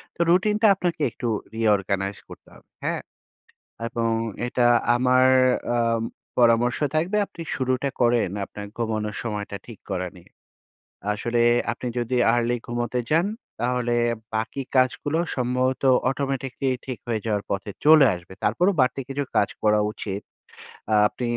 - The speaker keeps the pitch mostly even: No, average, 3.3 semitones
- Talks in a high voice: No, low, 120 Hz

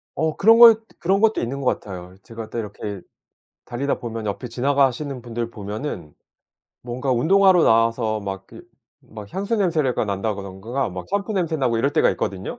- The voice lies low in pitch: Yes, low, 120 Hz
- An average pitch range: No, wide, 6.6 semitones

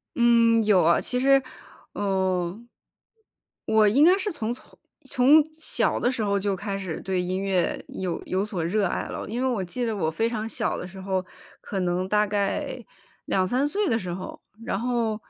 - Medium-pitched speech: No, high, 210 Hz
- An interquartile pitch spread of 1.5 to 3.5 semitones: No, average, 4.2 semitones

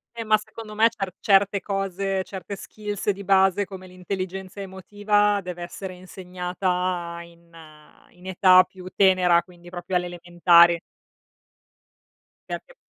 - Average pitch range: No, narrow, 1.9 semitones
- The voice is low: No, medium, 185 Hz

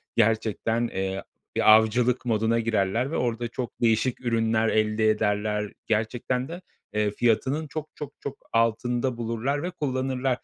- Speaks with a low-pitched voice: Yes, low, 115 Hz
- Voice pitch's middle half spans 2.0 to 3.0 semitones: Yes, average, 2.7 semitones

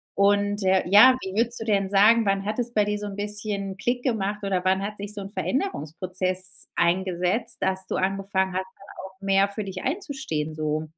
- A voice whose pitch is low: No, high, 195 Hz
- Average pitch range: No, narrow, 1.9 semitones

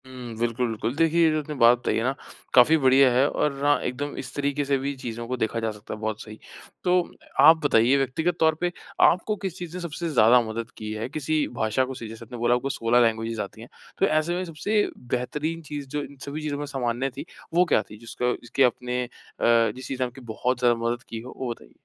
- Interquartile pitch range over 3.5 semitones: Yes, average, 4.1 semitones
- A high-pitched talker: No, low, 130 Hz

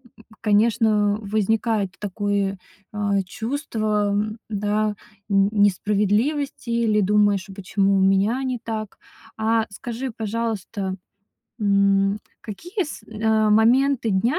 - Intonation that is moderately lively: No, narrow, 2.2 semitones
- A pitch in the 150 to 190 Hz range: No, high, 210 Hz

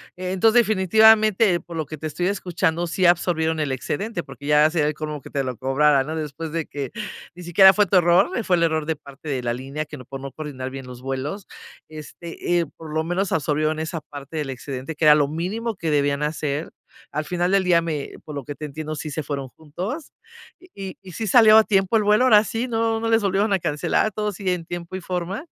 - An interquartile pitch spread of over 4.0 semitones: Yes, average, 4.4 semitones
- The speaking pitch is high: No, medium, 165 Hz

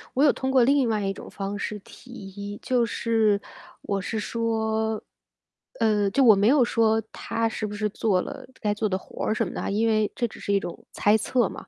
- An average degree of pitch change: No, narrow, 2.1 semitones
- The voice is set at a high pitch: Yes, high, 220 Hz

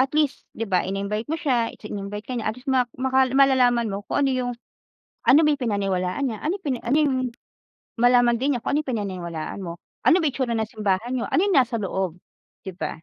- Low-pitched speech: No, high, 240 Hz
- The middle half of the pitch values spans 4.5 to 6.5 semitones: Yes, average, 4.8 semitones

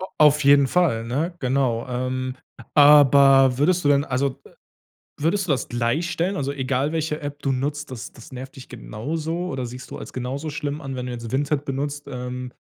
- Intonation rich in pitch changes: No, average, 2.8 semitones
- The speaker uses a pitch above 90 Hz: Yes, medium, 140 Hz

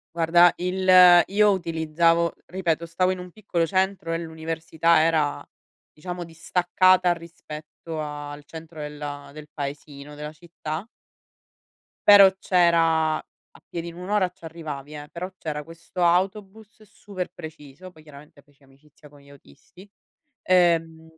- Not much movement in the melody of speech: No, average, 3.0 semitones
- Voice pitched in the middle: Yes, medium, 165 Hz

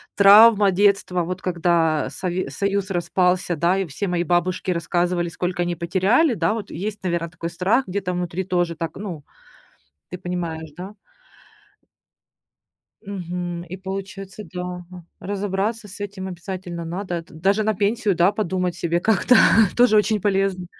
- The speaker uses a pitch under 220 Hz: Yes, medium, 185 Hz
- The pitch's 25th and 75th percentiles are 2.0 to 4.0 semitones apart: Yes, narrow, 2.4 semitones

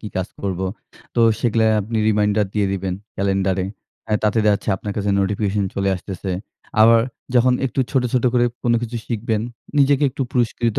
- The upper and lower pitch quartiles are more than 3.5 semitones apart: No, average, 3.2 semitones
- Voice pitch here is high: No, low, 105 Hz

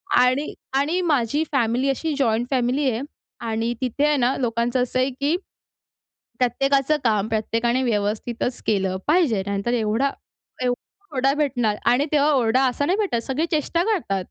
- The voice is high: Yes, very high, 255 Hz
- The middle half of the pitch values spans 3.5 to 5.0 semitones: Yes, average, 3.8 semitones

